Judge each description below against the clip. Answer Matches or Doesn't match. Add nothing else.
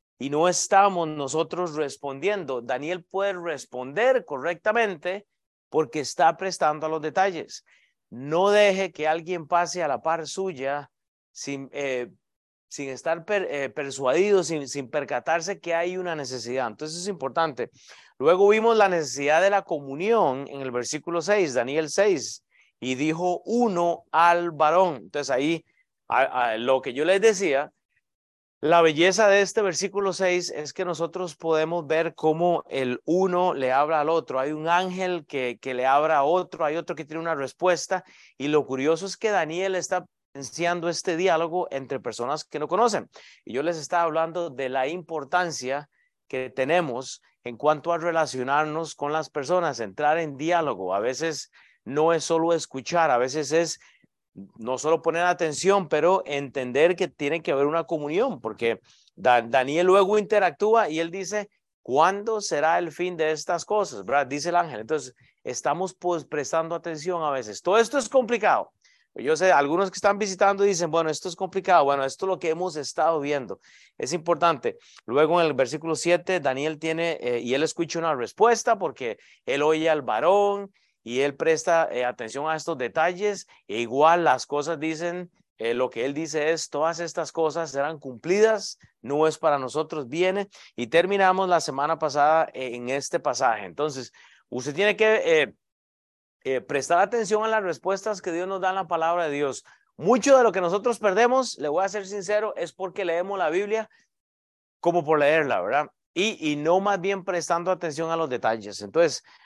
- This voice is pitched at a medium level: Matches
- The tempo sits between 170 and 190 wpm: Matches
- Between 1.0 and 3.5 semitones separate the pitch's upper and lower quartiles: Doesn't match